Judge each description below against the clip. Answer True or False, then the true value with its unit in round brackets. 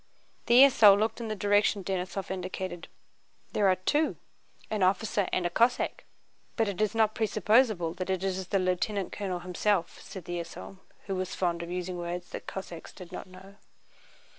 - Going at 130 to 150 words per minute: False (175 wpm)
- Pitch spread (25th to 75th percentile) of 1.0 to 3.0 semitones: True (2.6 semitones)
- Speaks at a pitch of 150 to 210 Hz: True (190 Hz)